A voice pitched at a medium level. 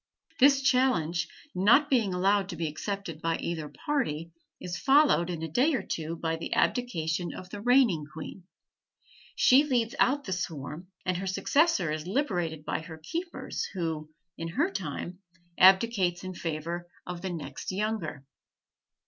Yes: medium, 180 Hz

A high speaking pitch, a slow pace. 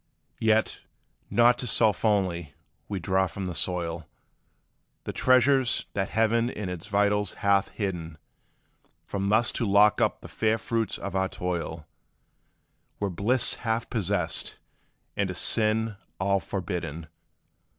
No: low, 100 Hz; slow, 130 wpm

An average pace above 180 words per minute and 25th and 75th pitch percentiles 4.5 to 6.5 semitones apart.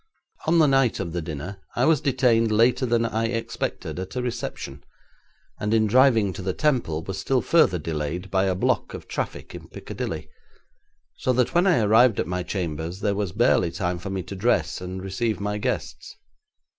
Yes: average, 190 wpm; average, 5.0 semitones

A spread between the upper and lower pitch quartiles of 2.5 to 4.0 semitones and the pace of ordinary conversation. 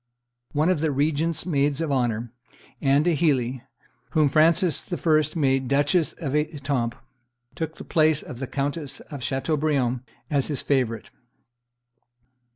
No: average, 2.9 semitones; slow, 130 wpm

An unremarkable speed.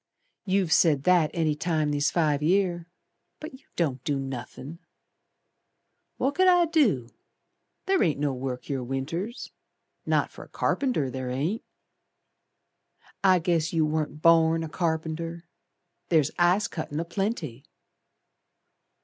No: slow, 130 wpm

